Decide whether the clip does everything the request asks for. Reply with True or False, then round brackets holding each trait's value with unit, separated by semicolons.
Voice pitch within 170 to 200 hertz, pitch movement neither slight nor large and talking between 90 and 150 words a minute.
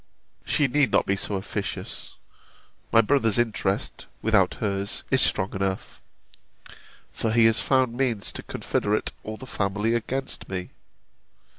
False (110 Hz; 3.4 semitones; 135 wpm)